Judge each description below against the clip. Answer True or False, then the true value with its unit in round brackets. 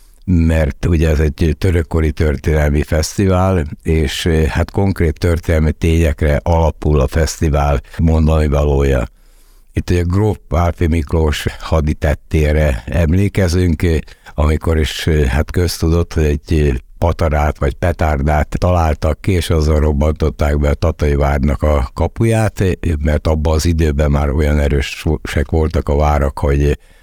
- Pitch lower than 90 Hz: True (80 Hz)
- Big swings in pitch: False (2.5 semitones)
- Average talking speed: True (120 wpm)